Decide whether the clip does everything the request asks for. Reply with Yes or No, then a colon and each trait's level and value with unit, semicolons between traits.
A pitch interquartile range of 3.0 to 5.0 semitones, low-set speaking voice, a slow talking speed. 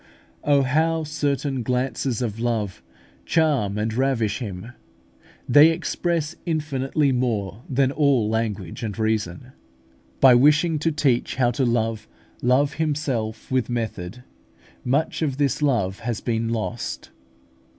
Yes: average, 4.4 semitones; low, 125 Hz; slow, 125 wpm